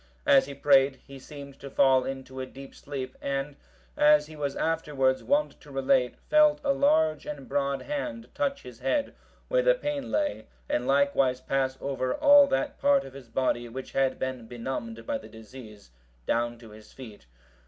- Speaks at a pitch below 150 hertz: Yes, low, 135 Hz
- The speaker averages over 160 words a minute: Yes, average, 180 wpm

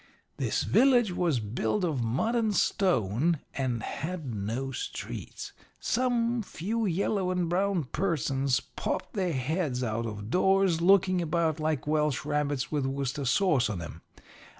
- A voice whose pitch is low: No, medium, 155 Hz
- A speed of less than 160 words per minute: Yes, average, 140 wpm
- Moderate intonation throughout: No, wide, 6.5 semitones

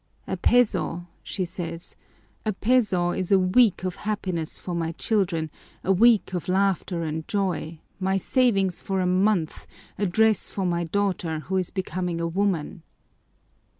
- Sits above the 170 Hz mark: Yes, medium, 185 Hz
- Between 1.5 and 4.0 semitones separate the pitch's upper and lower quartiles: Yes, average, 2.8 semitones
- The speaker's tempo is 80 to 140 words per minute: No, average, 150 wpm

